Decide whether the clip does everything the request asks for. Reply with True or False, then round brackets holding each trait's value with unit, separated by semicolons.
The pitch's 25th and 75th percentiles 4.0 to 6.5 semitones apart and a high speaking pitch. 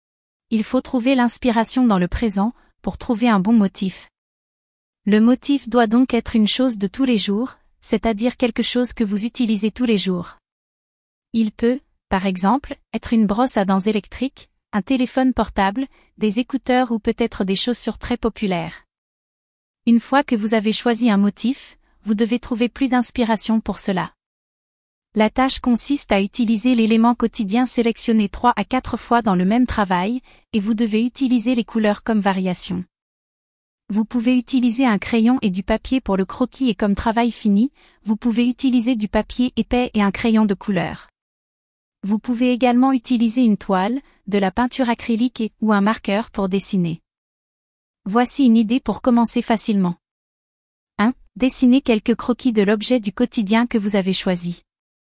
False (3.1 semitones; 230 Hz)